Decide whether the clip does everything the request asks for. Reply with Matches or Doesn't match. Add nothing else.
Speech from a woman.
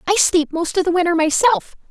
Matches